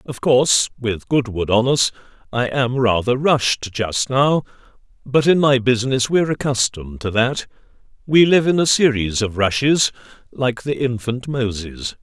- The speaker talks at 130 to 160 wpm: Yes, average, 150 wpm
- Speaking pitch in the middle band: No, low, 125 Hz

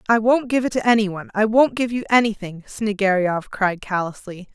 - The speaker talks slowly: No, average, 200 wpm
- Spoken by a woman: Yes, female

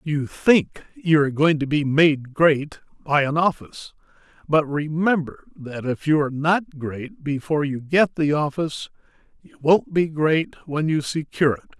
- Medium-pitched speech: Yes, medium, 150 Hz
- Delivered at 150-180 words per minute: Yes, average, 170 wpm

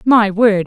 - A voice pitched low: No, high, 210 Hz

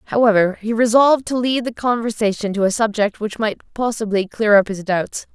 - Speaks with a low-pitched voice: No, high, 220 Hz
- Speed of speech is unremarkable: Yes, average, 190 wpm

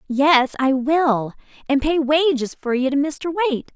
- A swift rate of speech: No, average, 175 wpm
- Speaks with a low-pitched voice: No, very high, 285 Hz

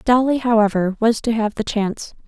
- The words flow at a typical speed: Yes, average, 185 wpm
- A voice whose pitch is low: No, high, 225 Hz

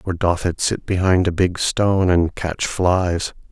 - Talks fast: No, average, 190 wpm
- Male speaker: Yes, male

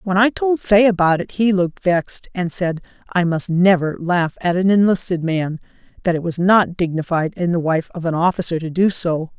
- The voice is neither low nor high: Yes, medium, 180 Hz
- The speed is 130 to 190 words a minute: No, fast, 205 wpm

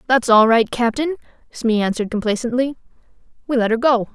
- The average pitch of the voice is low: No, high, 240 Hz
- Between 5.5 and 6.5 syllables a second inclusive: Yes, 6.2 syllables/s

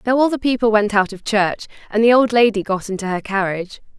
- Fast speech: Yes, fast, 240 wpm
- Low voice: No, high, 215 Hz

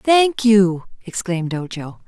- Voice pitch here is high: Yes, high, 200 Hz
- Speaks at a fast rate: No, slow, 115 wpm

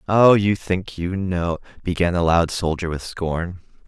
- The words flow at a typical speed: Yes, average, 170 wpm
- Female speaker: No, male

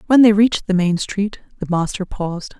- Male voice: No, female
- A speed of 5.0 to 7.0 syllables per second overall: Yes, 5.4 syllables/s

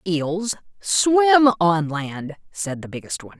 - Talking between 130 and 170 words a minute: Yes, average, 140 wpm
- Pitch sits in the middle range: Yes, medium, 180 Hz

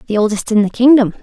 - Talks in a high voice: Yes, high, 225 Hz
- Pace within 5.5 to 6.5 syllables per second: Yes, 6.1 syllables/s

